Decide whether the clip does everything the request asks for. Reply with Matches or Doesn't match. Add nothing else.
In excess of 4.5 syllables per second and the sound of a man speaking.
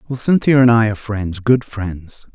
Matches